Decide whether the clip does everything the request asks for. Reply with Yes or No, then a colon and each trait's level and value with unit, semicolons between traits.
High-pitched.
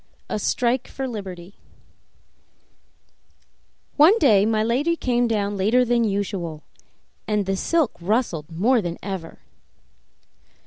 Yes: high, 215 Hz